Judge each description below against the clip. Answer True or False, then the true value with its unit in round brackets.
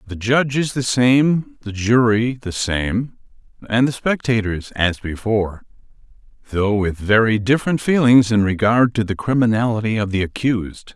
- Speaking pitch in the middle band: False (115 Hz)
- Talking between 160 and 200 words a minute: False (150 wpm)